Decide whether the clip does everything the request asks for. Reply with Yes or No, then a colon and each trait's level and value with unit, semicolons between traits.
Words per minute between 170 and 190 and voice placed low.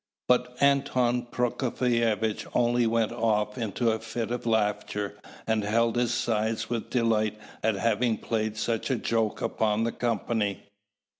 No: average, 140 wpm; low, 115 Hz